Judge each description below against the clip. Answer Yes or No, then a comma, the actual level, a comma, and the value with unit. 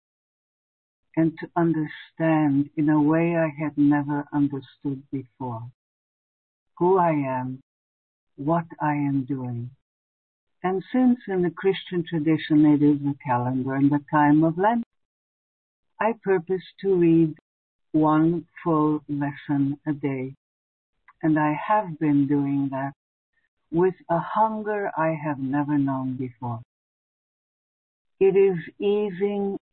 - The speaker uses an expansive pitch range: No, average, 3.8 semitones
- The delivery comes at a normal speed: No, slow, 120 wpm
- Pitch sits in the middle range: Yes, medium, 150 Hz